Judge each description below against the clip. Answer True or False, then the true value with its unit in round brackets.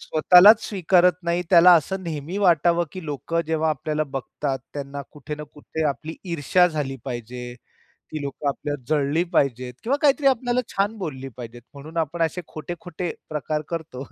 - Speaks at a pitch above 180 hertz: False (155 Hz)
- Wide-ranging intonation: False (3.9 semitones)